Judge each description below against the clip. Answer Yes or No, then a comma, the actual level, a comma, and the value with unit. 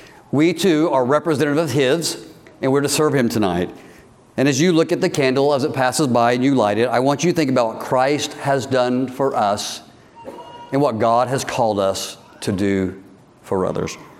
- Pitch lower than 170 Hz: Yes, low, 135 Hz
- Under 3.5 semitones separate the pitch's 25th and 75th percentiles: No, average, 4.1 semitones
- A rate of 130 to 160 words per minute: No, fast, 205 wpm